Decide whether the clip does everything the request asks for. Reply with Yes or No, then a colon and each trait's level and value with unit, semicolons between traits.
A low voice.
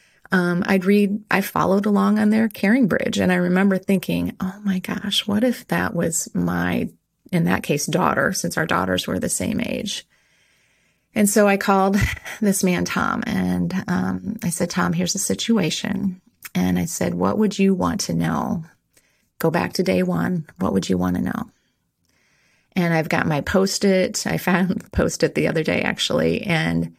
No: high, 190 Hz